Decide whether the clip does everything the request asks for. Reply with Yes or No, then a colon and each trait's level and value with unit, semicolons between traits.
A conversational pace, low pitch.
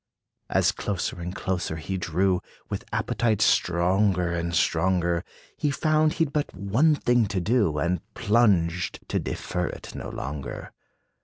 Yes: average, 145 wpm; very low, 95 Hz